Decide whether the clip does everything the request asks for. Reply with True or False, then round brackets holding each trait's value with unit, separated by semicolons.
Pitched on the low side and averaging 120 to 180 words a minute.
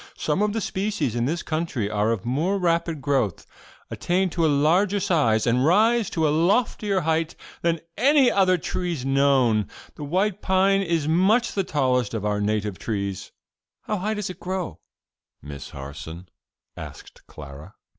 False (160 Hz; 160 wpm)